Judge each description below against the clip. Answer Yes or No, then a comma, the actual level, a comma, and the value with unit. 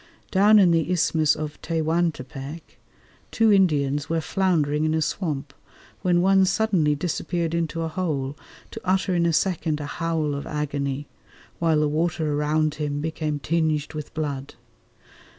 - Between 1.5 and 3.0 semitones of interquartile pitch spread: Yes, average, 2.7 semitones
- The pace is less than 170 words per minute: Yes, average, 150 wpm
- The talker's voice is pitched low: No, medium, 155 Hz